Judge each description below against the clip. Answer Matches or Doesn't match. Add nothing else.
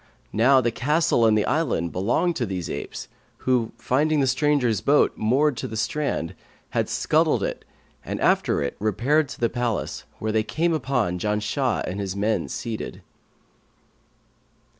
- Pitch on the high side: Doesn't match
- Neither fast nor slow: Matches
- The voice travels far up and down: Doesn't match